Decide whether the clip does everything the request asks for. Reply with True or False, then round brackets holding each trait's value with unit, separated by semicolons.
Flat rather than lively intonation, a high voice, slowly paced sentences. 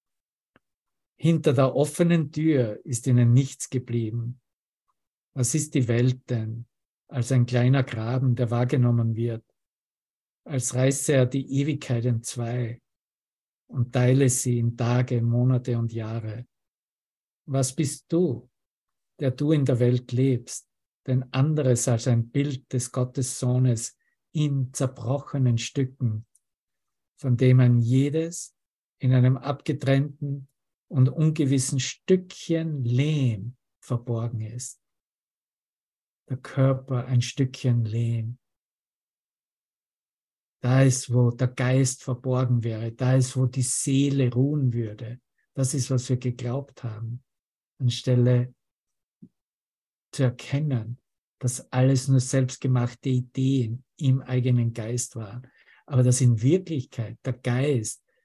False (2.0 semitones; 130 Hz; 115 wpm)